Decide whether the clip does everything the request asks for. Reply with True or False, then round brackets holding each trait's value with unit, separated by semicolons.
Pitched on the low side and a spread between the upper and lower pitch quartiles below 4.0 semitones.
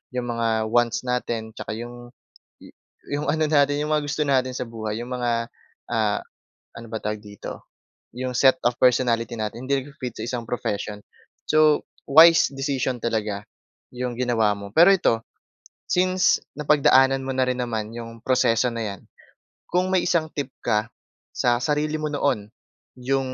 True (125 Hz; 3.6 semitones)